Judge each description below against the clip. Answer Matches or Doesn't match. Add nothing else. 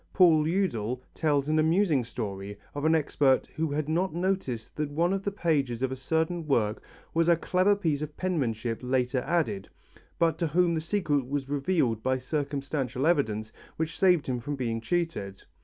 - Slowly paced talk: Doesn't match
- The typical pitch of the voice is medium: Matches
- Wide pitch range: Doesn't match